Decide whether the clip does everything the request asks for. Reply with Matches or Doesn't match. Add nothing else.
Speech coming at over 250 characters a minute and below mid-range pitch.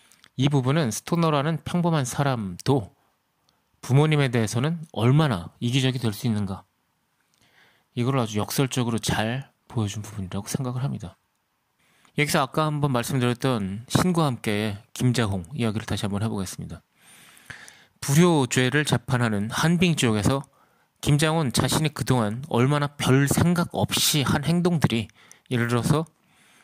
Matches